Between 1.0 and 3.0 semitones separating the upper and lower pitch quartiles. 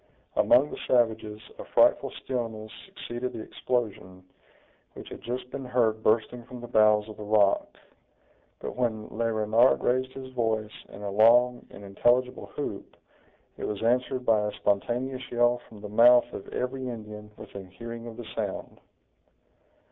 Yes: narrow, 2.5 semitones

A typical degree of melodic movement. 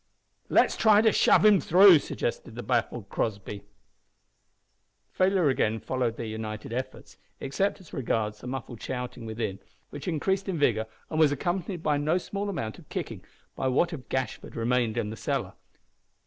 No: wide, 7.4 semitones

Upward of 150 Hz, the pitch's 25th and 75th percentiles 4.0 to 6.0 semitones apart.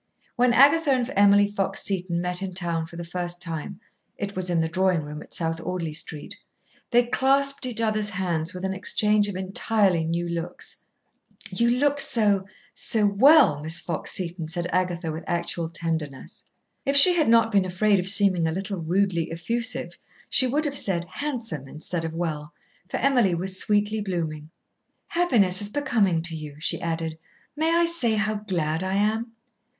Yes: high, 190 Hz; average, 5.0 semitones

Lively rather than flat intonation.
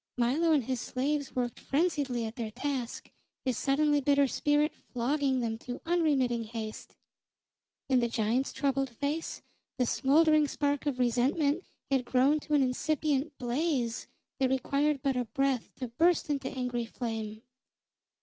No: average, 3.2 semitones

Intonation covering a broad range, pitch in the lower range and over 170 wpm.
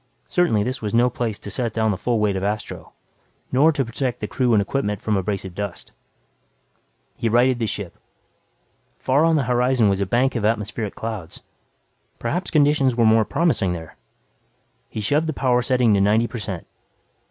No: average, 3.9 semitones; low, 115 Hz; average, 180 wpm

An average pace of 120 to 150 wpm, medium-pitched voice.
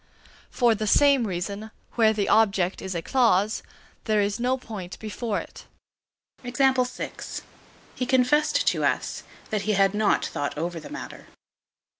No: average, 140 wpm; high, 215 Hz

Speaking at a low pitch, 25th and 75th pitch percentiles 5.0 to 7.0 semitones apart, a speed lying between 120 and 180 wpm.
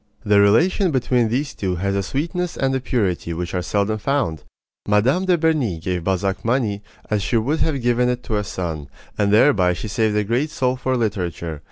No: low, 110 Hz; wide, 5.4 semitones; average, 200 wpm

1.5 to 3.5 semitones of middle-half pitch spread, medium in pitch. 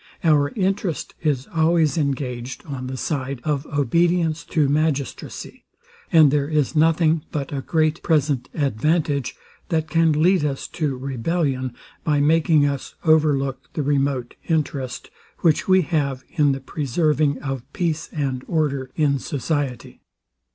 Yes: average, 2.8 semitones; medium, 150 Hz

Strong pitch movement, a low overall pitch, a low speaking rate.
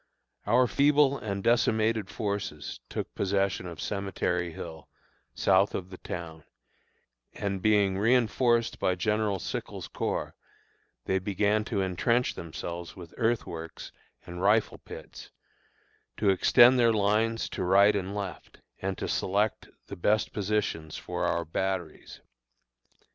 No: average, 3.3 semitones; low, 100 Hz; slow, 125 wpm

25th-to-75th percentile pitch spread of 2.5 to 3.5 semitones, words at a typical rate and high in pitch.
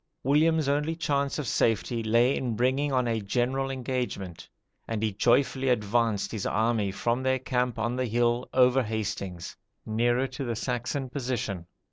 No: average, 2.9 semitones; average, 155 wpm; low, 120 Hz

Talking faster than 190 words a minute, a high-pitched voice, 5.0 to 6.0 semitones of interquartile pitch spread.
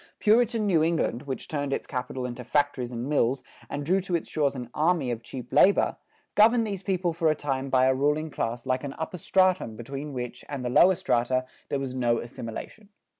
No: fast, 205 wpm; medium, 140 Hz; average, 5.3 semitones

